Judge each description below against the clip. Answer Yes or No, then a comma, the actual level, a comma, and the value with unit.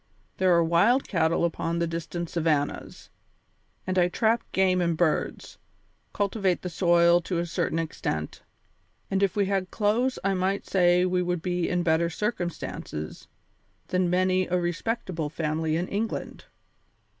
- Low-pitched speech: No, medium, 175 Hz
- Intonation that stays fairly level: Yes, narrow, 2.2 semitones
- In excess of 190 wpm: No, average, 145 wpm